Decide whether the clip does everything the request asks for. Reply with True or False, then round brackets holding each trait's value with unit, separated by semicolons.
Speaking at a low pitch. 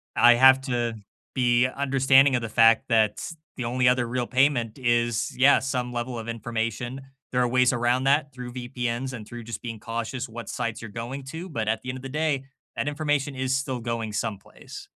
True (125 Hz)